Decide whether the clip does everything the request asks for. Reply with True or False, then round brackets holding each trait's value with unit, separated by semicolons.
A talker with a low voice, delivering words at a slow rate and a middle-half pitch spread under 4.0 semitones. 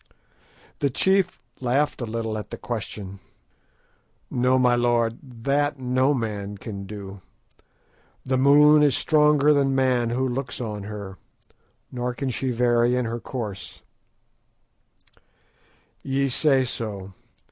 True (125 Hz; 125 wpm; 3.4 semitones)